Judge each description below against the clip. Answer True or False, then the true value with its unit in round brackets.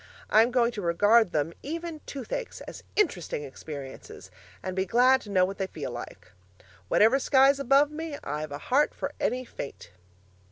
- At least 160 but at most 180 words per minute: True (165 wpm)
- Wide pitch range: True (7.6 semitones)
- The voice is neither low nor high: False (235 Hz)